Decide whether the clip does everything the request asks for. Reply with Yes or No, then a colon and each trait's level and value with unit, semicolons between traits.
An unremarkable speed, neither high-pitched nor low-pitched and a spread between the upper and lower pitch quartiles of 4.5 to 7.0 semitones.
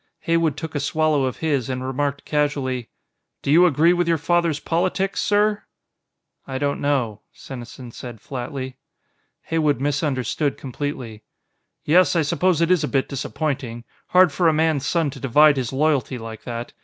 No: average, 160 wpm; medium, 145 Hz; average, 3.8 semitones